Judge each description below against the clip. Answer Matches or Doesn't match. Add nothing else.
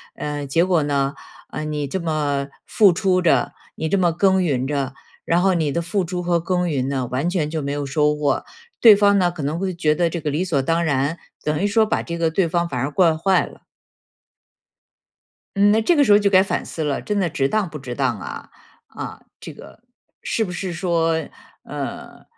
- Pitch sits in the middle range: Matches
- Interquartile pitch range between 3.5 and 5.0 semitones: Matches